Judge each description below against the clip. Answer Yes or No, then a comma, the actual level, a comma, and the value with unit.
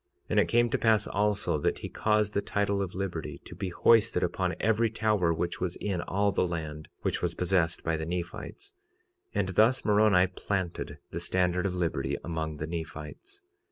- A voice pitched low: Yes, very low, 95 Hz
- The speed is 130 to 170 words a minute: No, average, 190 wpm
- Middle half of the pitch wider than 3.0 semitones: Yes, average, 3.7 semitones